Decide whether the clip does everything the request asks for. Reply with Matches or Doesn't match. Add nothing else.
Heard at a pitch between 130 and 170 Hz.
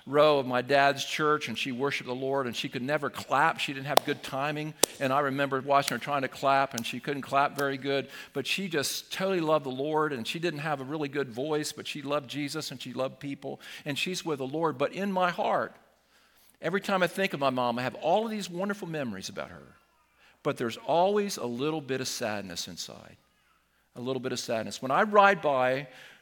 Matches